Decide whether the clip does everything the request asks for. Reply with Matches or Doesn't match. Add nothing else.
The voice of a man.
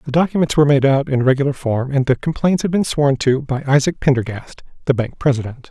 Matches